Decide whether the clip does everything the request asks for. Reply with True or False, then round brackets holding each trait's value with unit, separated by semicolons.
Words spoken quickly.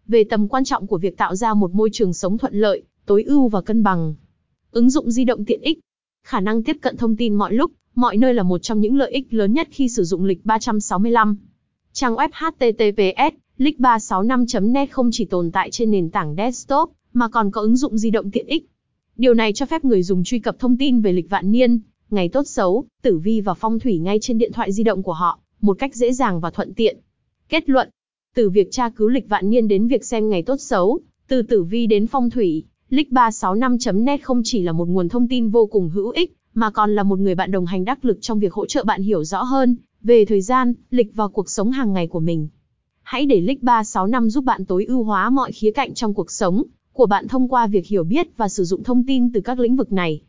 False (235 wpm)